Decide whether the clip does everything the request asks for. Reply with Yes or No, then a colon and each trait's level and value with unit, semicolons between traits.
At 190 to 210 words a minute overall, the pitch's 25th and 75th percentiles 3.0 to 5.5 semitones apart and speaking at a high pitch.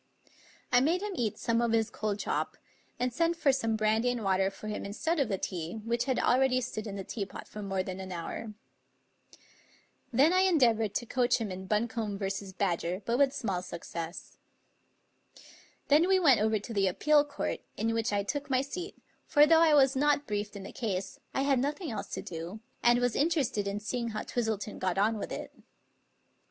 Yes: fast, 205 wpm; average, 5.1 semitones; high, 225 Hz